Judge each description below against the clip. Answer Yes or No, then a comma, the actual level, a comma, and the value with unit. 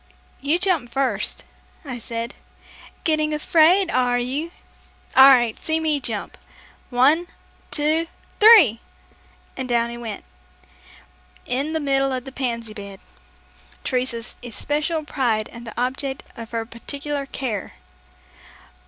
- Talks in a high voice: Yes, very high, 265 Hz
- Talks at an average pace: No, slow, 120 wpm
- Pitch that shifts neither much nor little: Yes, average, 4.3 semitones